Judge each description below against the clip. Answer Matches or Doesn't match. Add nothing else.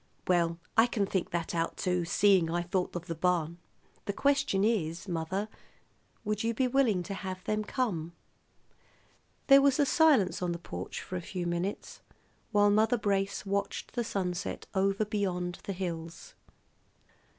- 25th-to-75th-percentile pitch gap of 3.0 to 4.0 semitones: Matches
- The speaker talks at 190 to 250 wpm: Doesn't match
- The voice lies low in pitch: Doesn't match